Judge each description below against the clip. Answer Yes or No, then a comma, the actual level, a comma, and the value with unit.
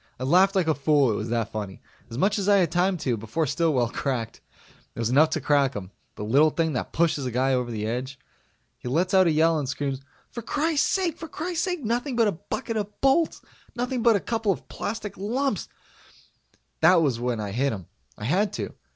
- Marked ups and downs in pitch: Yes, wide, 8.7 semitones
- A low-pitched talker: No, medium, 160 Hz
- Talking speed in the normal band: No, fast, 220 wpm